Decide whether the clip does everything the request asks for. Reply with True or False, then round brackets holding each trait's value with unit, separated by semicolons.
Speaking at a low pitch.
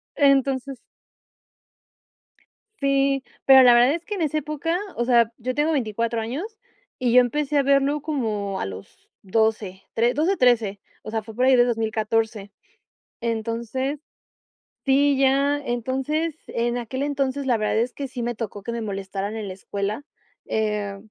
False (245 Hz)